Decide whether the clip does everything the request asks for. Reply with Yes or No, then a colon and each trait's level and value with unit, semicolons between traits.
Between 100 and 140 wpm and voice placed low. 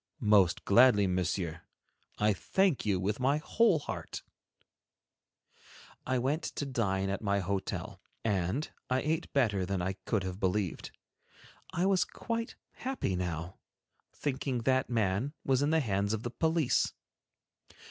Yes: slow, 135 wpm; low, 110 Hz